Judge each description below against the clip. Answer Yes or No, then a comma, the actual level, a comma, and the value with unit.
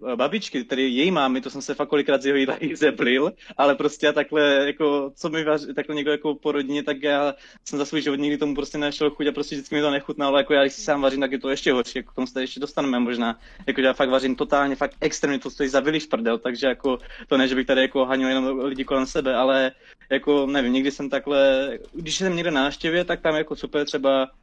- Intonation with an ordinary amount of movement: No, narrow, 1.7 semitones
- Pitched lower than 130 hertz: No, medium, 140 Hz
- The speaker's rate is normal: No, fast, 255 wpm